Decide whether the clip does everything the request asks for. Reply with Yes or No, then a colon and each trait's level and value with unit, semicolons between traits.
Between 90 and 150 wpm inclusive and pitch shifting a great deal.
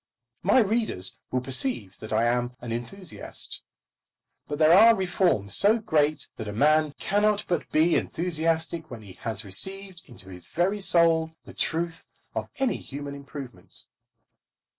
Yes: average, 145 wpm; wide, 7.5 semitones